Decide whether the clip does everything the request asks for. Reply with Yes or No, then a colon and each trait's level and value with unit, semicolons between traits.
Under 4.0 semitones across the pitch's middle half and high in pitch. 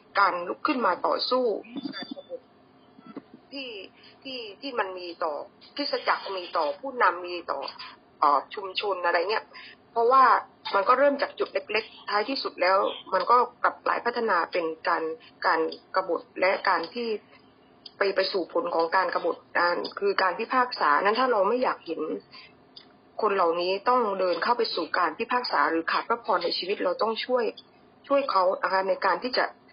No: wide, 5.6 semitones; high, 215 Hz